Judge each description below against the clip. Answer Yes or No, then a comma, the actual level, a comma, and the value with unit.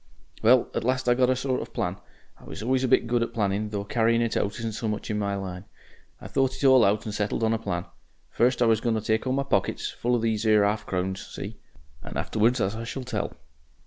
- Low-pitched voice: Yes, low, 115 Hz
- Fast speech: Yes, fast, 250 wpm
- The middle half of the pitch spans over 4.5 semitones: No, average, 2.9 semitones